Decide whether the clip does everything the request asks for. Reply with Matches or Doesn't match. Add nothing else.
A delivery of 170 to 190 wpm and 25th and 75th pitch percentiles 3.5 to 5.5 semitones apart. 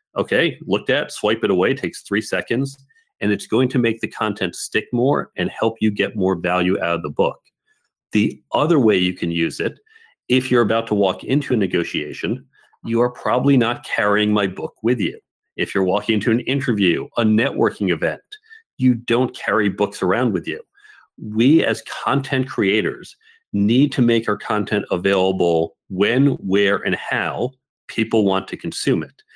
Matches